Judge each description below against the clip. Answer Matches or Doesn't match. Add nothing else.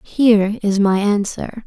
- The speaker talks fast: Doesn't match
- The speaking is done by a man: Doesn't match